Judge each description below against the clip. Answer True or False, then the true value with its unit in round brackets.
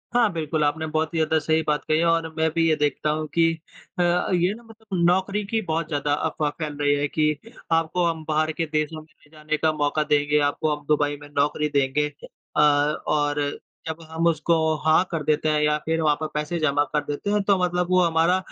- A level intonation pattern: True (2.0 semitones)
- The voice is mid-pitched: True (155 Hz)